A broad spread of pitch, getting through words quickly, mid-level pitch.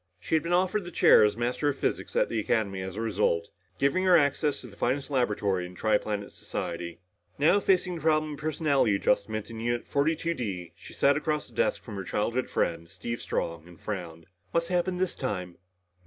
No: wide, 7.8 semitones; fast, 210 wpm; low, 120 Hz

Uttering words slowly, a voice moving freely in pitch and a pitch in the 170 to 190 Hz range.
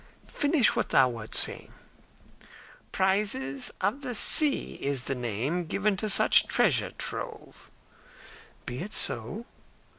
Yes: slow, 120 wpm; wide, 8.8 semitones; medium, 185 Hz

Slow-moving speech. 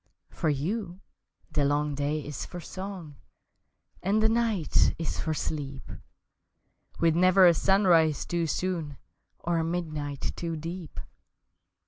Yes: slow, 125 wpm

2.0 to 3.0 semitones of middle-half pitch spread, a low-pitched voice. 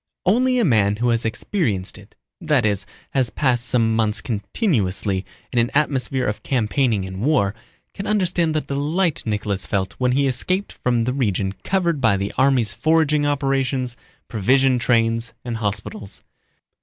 No: wide, 5.4 semitones; low, 125 Hz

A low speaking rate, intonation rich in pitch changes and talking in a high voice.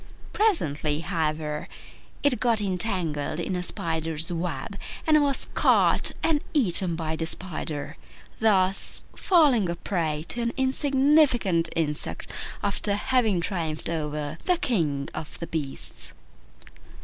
No: slow, 120 wpm; wide, 6.9 semitones; medium, 175 Hz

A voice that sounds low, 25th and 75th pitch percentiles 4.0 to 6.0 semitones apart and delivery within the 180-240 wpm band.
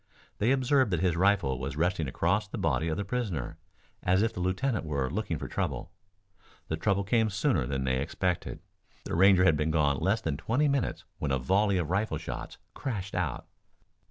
Yes: very low, 90 Hz; wide, 5.4 semitones; average, 190 wpm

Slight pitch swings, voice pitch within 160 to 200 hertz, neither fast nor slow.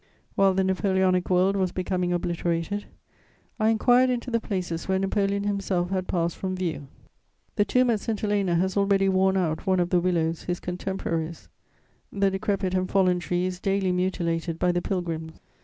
Yes: narrow, 1.9 semitones; medium, 185 Hz; average, 175 wpm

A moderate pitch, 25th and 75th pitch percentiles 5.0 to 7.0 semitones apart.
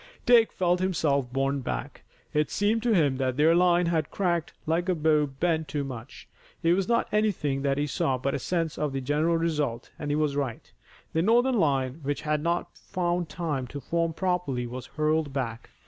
No: medium, 155 Hz; average, 4.1 semitones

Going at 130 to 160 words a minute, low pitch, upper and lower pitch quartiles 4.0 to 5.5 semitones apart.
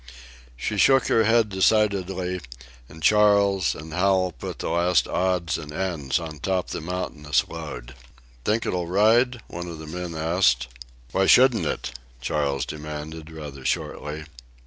Yes: average, 145 wpm; very low, 90 Hz; average, 4.3 semitones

